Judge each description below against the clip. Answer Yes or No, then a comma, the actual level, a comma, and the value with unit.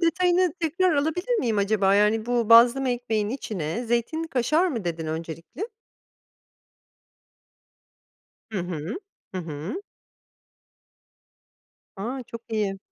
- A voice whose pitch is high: Yes, high, 230 Hz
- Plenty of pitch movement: Yes, wide, 7.4 semitones